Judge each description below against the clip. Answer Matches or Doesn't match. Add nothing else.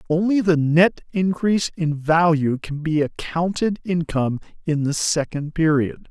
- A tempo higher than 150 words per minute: Doesn't match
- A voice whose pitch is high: Doesn't match